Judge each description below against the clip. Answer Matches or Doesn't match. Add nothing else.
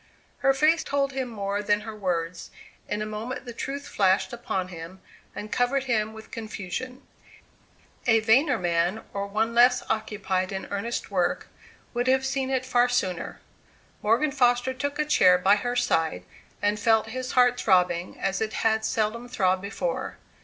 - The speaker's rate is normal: Matches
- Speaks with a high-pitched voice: Matches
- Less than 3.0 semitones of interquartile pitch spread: Doesn't match